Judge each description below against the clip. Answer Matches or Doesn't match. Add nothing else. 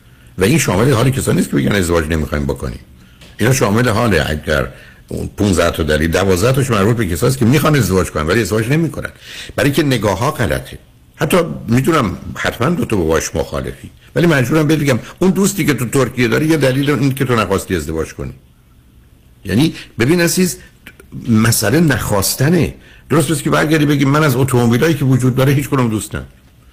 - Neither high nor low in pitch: Doesn't match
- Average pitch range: Doesn't match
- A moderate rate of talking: Doesn't match